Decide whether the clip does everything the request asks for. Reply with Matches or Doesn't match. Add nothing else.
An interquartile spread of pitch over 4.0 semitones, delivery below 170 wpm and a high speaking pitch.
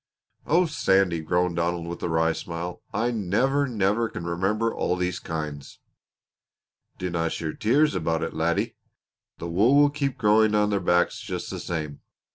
Doesn't match